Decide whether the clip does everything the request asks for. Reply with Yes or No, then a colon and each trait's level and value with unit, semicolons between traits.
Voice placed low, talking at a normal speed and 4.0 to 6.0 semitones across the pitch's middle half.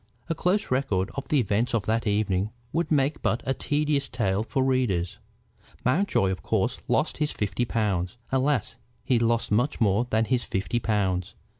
Yes: low, 115 Hz; average, 170 wpm; average, 4.7 semitones